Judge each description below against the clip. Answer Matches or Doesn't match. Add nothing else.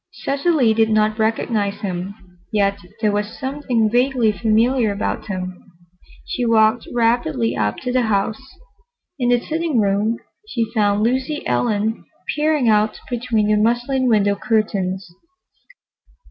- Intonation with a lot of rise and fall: Doesn't match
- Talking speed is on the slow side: Matches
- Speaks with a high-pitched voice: Matches